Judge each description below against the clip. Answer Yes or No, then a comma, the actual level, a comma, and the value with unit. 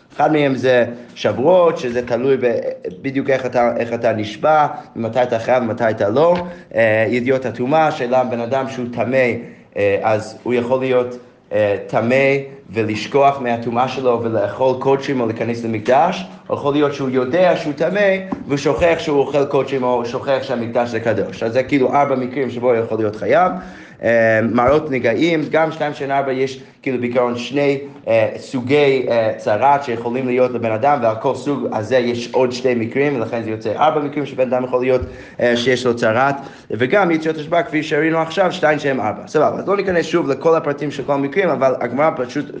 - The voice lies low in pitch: Yes, low, 130 Hz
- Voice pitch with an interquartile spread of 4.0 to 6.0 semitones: No, average, 3.4 semitones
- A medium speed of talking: No, fast, 180 wpm